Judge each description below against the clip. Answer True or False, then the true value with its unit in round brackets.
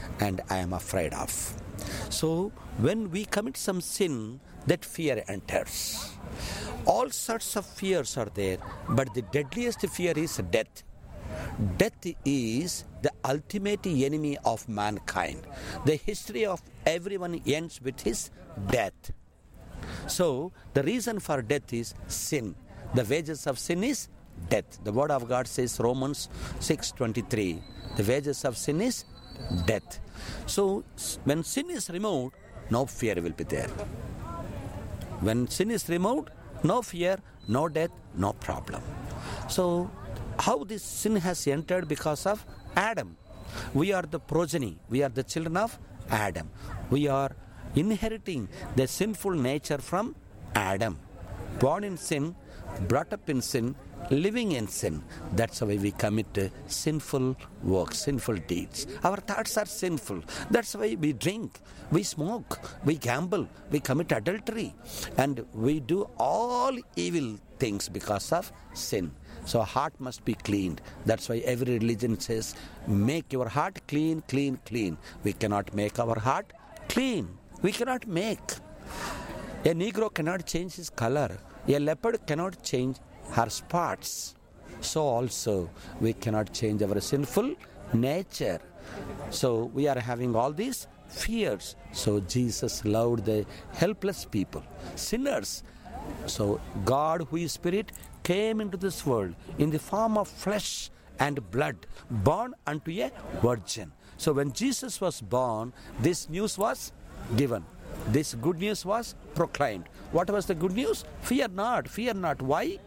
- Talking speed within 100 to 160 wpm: True (135 wpm)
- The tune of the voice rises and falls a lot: True (8.7 semitones)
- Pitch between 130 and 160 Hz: True (135 Hz)